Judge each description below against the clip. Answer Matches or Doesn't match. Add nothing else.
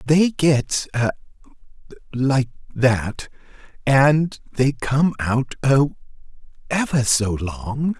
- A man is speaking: Matches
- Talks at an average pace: Doesn't match